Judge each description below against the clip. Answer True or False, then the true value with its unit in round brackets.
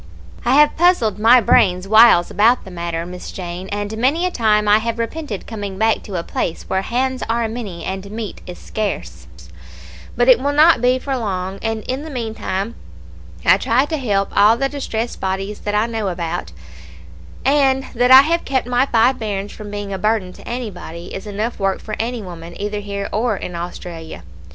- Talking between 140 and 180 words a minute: False (195 wpm)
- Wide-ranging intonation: False (4.2 semitones)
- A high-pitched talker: True (215 Hz)